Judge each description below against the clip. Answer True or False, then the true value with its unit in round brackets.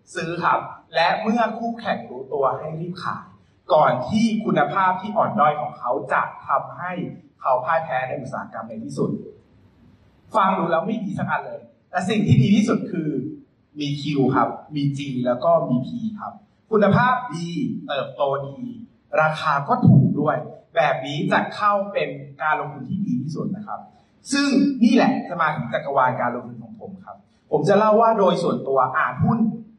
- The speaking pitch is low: False (185 Hz)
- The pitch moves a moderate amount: False (7.2 semitones)